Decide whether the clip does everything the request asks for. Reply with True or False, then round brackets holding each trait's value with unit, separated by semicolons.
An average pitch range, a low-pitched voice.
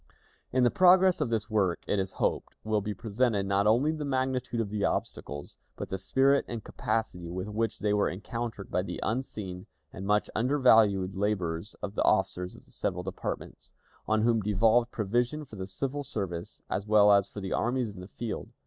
True (3.8 semitones; 105 Hz)